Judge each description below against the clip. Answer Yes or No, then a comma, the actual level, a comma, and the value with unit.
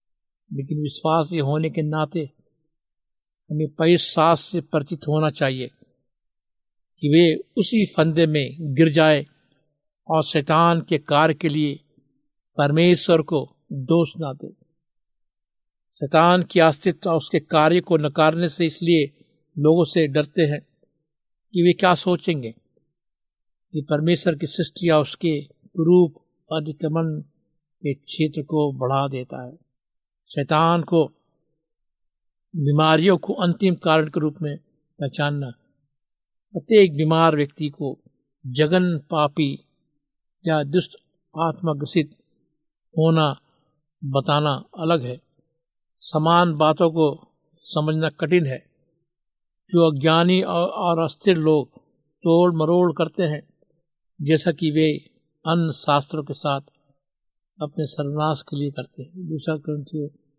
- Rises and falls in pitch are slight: Yes, narrow, 2.1 semitones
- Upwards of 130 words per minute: No, average, 115 wpm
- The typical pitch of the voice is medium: Yes, medium, 155 Hz